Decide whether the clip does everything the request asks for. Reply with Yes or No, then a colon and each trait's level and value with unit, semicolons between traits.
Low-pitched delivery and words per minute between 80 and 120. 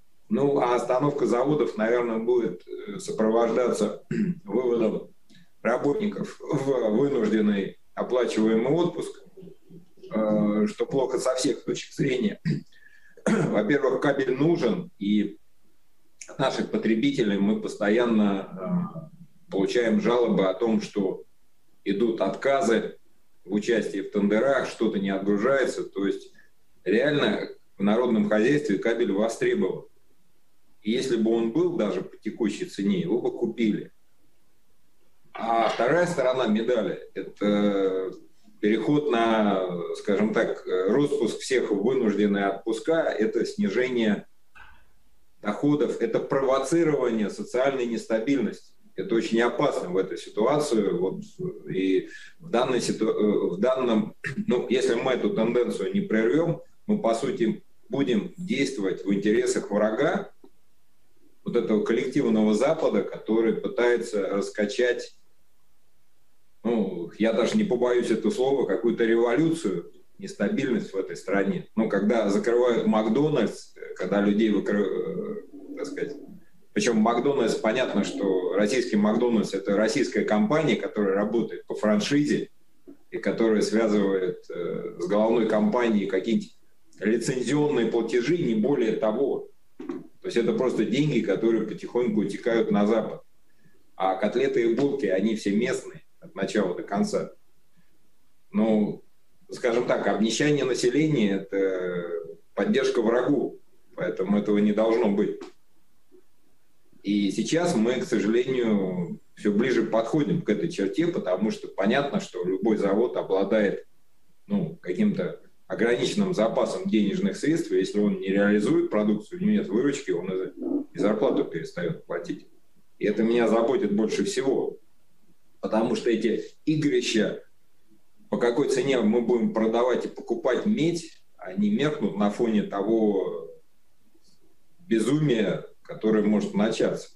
Yes: low, 120 Hz; average, 115 wpm